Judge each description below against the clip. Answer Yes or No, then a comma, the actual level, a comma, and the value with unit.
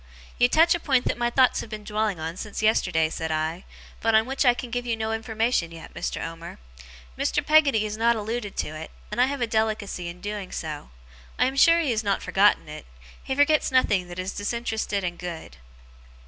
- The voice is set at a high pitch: Yes, high, 220 Hz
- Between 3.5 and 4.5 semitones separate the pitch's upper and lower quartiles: No, wide, 5.4 semitones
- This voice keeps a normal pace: No, fast, 215 wpm